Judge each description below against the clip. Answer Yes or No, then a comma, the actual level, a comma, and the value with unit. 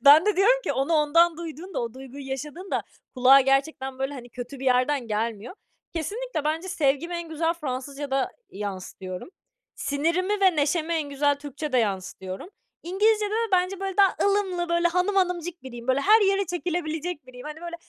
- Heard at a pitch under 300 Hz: No, very high, 310 Hz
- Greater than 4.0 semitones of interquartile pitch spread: Yes, average, 5.2 semitones